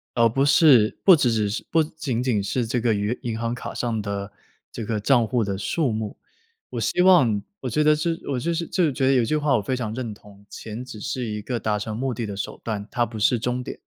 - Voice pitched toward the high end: No, low, 120 Hz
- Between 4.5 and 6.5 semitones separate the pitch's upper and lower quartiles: No, average, 3.9 semitones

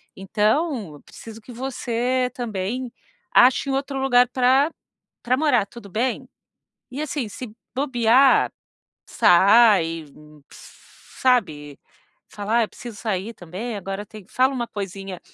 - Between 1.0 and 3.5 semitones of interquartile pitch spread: No, average, 4.2 semitones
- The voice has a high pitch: Yes, high, 235 Hz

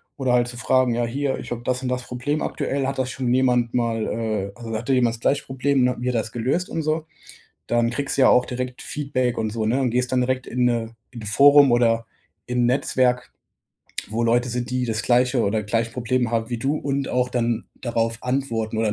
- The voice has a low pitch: Yes, low, 125 Hz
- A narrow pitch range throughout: Yes, narrow, 1.8 semitones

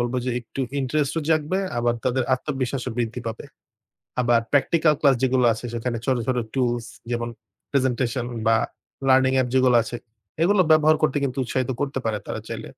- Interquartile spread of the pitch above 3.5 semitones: No, narrow, 2.5 semitones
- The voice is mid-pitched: No, low, 130 Hz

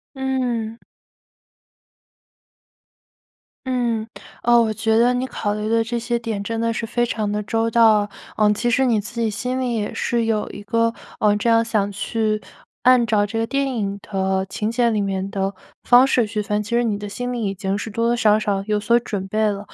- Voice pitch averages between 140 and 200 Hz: No, high, 225 Hz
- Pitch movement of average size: No, narrow, 2.3 semitones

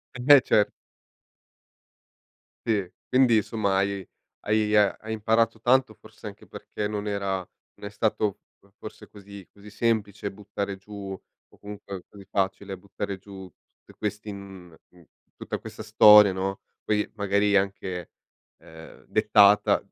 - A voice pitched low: Yes, low, 100 Hz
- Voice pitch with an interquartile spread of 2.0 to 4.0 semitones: No, narrow, 1.5 semitones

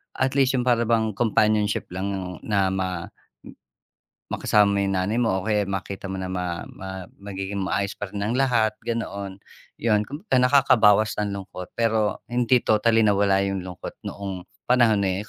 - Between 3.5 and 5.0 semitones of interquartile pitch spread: No, average, 3.0 semitones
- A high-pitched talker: No, low, 105 Hz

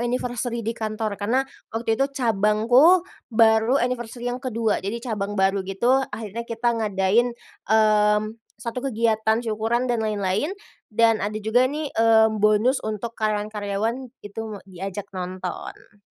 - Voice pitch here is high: Yes, high, 220 Hz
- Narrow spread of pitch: Yes, narrow, 2.3 semitones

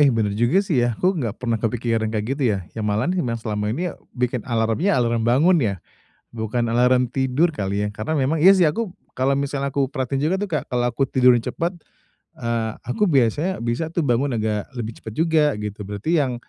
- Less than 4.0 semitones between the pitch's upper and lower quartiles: No, average, 4.9 semitones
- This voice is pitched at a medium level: No, low, 125 Hz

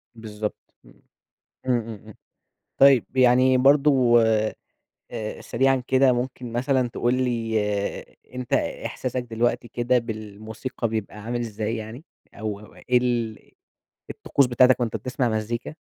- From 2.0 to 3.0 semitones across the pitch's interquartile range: Yes, narrow, 2.4 semitones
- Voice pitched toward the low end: Yes, low, 120 Hz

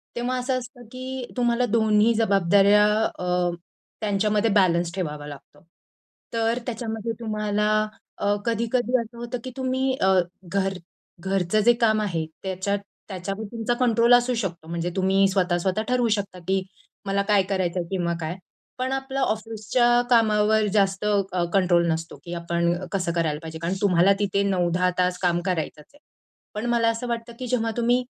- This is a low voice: No, high, 205 Hz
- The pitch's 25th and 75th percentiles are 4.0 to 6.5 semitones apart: Yes, average, 4.3 semitones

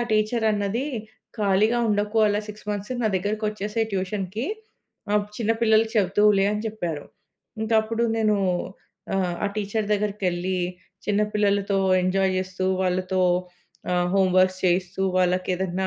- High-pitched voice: Yes, high, 200 Hz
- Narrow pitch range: Yes, narrow, 2.3 semitones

